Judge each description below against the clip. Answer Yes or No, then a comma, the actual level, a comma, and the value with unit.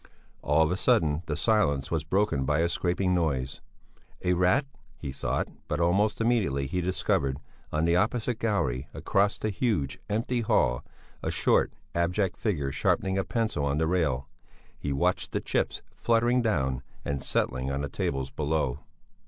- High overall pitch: No, very low, 85 Hz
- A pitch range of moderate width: No, wide, 6.7 semitones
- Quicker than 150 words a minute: Yes, average, 160 wpm